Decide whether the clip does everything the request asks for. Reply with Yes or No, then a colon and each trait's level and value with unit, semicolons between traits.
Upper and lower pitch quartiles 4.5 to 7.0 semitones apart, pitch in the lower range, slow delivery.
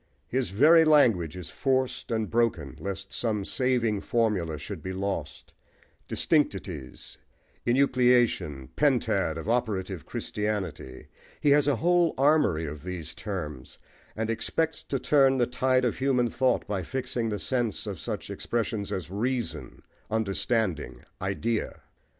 Yes: wide, 5.6 semitones; low, 110 Hz; slow, 130 wpm